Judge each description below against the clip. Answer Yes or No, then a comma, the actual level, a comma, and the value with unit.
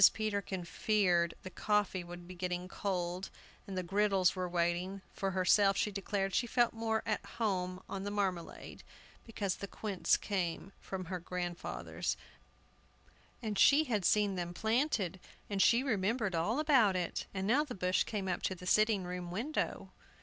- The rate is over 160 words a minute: No, average, 155 wpm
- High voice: Yes, high, 195 Hz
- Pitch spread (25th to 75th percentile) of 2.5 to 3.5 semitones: Yes, average, 2.8 semitones